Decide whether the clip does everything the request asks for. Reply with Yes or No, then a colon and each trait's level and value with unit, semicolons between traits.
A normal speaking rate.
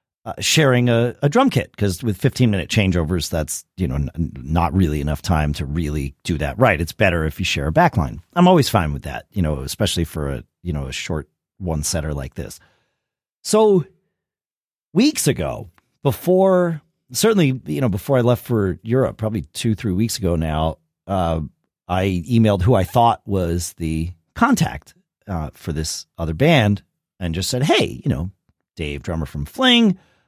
Yes: average, 180 wpm